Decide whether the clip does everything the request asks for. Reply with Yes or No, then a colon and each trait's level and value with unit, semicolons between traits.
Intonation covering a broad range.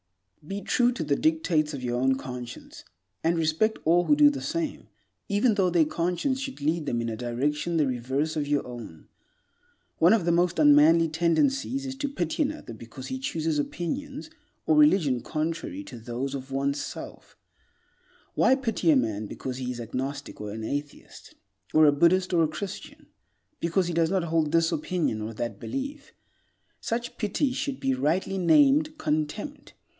Yes: wide, 8.4 semitones